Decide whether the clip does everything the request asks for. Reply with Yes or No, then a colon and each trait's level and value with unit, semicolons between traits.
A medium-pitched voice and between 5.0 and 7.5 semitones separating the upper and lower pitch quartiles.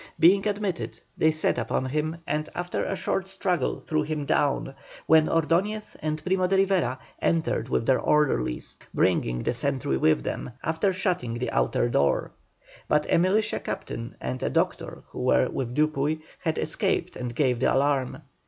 Yes: medium, 155 Hz; wide, 5.5 semitones